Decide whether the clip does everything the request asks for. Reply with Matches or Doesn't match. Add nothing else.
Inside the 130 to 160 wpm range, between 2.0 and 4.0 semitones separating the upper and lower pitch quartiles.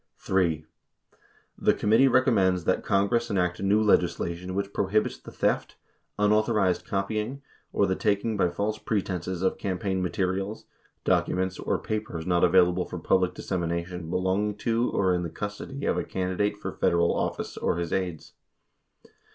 Matches